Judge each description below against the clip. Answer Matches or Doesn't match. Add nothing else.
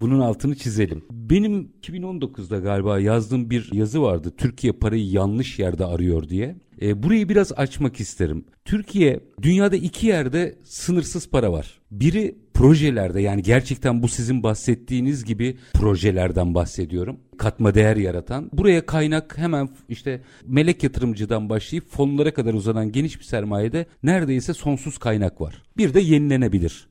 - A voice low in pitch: Matches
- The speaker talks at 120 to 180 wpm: Matches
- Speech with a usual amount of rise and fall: Doesn't match